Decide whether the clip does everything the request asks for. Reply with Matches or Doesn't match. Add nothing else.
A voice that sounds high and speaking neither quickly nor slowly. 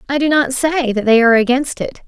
Doesn't match